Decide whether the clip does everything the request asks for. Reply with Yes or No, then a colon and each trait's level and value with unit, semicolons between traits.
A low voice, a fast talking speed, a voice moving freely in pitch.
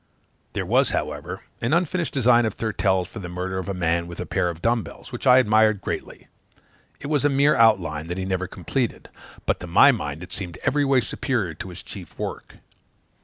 Yes: low, 100 Hz; fast, 210 wpm; wide, 6.1 semitones